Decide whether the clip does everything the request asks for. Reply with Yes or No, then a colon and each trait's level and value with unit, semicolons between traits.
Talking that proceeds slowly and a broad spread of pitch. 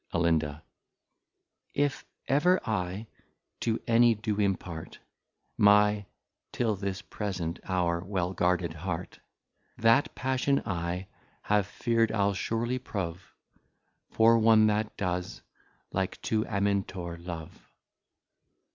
No: slow, 100 wpm; average, 4.0 semitones